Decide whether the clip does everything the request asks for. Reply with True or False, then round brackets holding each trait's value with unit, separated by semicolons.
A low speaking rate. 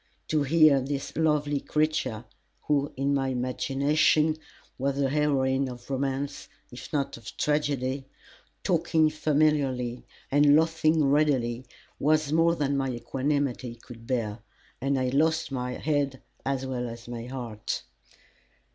True (130 wpm)